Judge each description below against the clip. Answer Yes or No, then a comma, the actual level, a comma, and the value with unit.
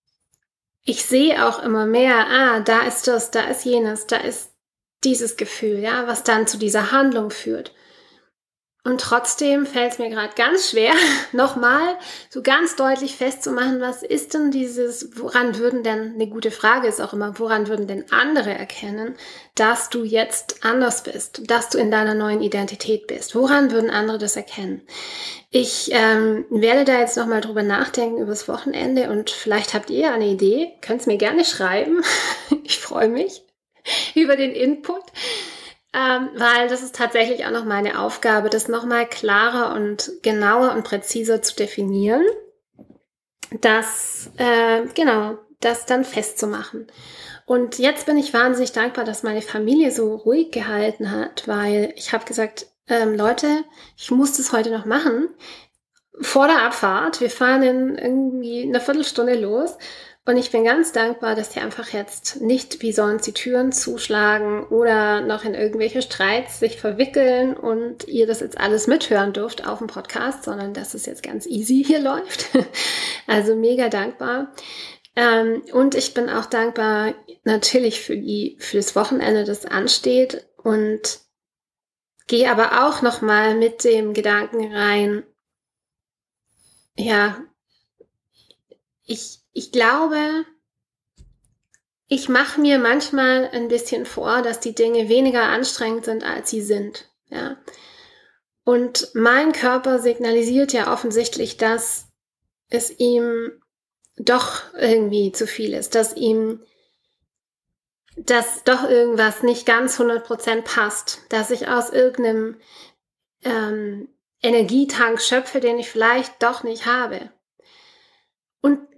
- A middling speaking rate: Yes, average, 140 wpm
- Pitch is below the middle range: No, high, 235 Hz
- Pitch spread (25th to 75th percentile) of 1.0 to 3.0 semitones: Yes, average, 2.7 semitones